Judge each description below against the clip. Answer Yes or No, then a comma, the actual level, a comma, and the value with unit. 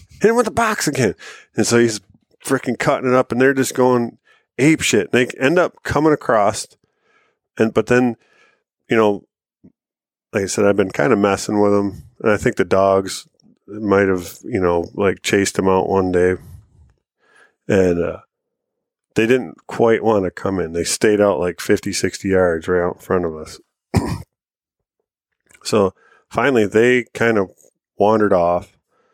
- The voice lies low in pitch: Yes, low, 100 Hz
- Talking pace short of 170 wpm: No, average, 175 wpm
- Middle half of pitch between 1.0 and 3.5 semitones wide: No, average, 3.9 semitones